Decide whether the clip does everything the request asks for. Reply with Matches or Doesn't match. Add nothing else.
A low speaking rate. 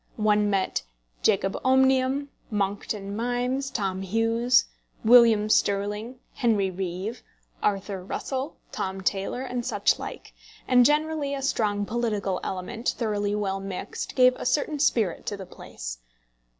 Matches